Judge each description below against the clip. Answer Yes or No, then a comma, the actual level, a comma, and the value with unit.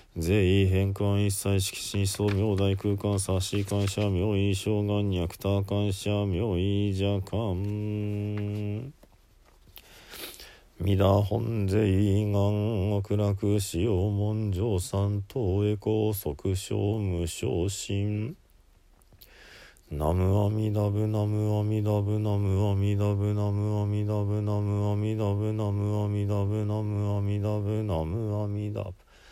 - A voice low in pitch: Yes, low, 105 Hz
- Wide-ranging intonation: No, narrow, 1.0 semitones